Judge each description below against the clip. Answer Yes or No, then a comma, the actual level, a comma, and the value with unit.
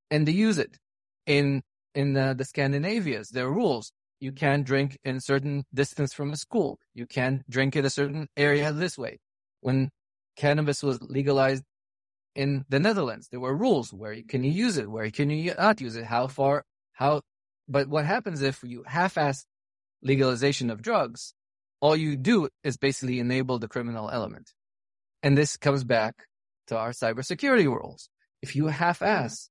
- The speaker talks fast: No, average, 170 wpm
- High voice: No, low, 135 Hz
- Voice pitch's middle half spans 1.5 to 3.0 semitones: Yes, narrow, 2.5 semitones